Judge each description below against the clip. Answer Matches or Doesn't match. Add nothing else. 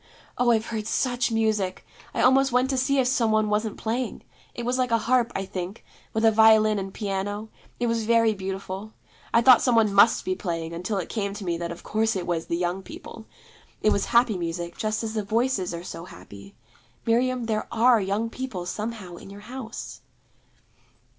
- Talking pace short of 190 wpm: Doesn't match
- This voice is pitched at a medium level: Doesn't match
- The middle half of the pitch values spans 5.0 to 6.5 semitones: Doesn't match